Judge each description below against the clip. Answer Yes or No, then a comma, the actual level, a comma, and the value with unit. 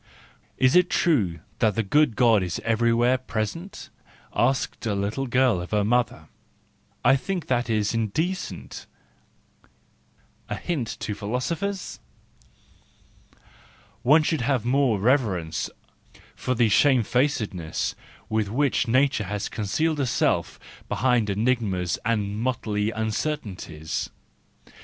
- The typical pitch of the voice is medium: No, low, 115 Hz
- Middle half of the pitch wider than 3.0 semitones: Yes, average, 4.4 semitones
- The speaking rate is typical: No, slow, 120 wpm